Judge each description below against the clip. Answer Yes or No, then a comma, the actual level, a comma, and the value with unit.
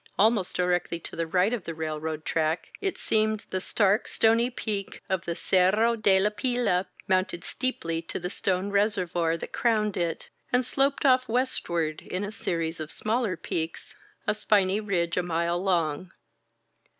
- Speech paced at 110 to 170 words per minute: Yes, average, 160 wpm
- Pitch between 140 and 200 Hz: Yes, high, 190 Hz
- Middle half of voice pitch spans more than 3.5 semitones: Yes, average, 4.3 semitones